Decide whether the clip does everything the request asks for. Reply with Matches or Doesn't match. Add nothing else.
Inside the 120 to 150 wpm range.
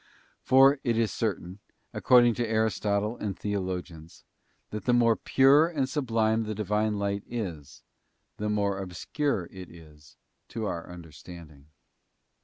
Matches